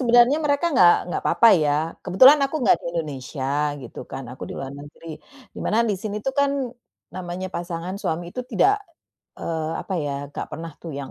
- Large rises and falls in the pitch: Yes, wide, 7.1 semitones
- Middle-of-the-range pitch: Yes, medium, 175 Hz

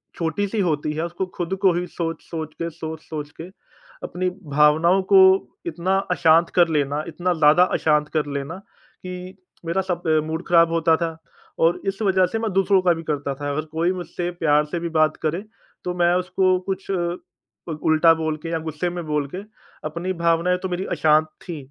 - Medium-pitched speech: Yes, medium, 170 Hz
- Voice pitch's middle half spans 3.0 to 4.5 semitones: No, narrow, 2.5 semitones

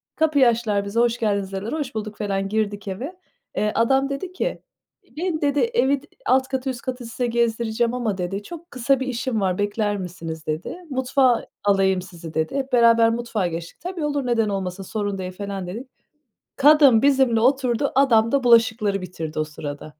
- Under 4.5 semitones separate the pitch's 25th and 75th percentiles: No, average, 5.0 semitones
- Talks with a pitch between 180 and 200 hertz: No, high, 230 Hz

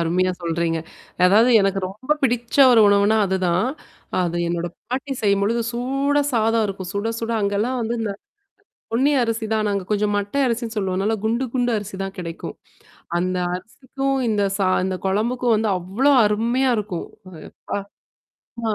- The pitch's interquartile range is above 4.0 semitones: No, average, 3.7 semitones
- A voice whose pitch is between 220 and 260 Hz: No, high, 210 Hz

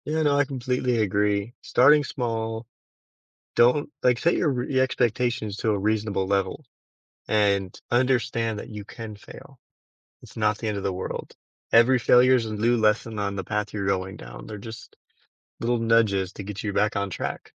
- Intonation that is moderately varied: Yes, average, 3.2 semitones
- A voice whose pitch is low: Yes, low, 110 Hz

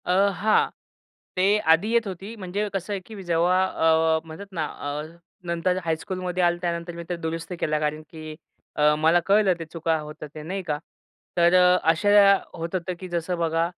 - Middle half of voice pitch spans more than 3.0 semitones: No, narrow, 2.5 semitones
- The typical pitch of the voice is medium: Yes, medium, 175 Hz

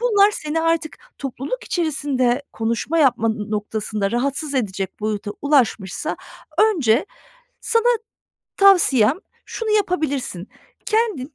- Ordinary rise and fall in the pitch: No, wide, 7.3 semitones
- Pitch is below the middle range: No, very high, 275 Hz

